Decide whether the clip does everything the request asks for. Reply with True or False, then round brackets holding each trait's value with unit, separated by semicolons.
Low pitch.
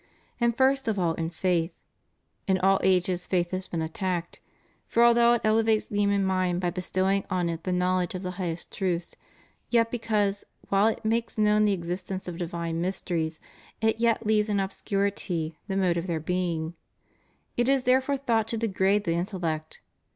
False (190 Hz)